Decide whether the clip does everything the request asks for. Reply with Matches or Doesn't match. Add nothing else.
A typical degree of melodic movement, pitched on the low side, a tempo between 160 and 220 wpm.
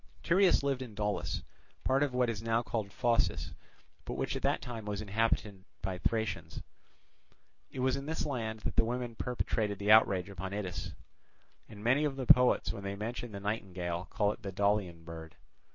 Matches